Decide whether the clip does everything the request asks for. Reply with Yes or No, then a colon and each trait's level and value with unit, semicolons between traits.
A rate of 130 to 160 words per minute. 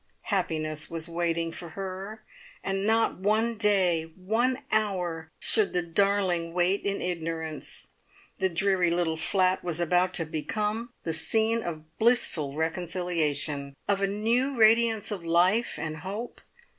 Yes: slow, 135 wpm